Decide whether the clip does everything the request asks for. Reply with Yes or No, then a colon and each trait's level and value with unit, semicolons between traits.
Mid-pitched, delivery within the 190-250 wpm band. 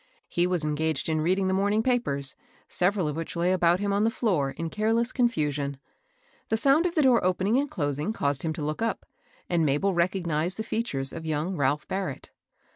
Yes: medium, 180 Hz; average, 200 wpm